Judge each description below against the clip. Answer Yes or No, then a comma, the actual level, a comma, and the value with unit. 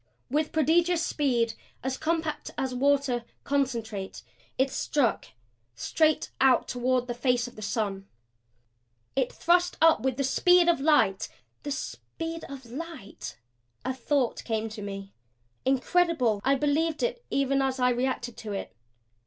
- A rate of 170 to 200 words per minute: No, average, 140 wpm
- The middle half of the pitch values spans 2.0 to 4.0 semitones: No, average, 4.4 semitones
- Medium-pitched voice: No, very high, 265 Hz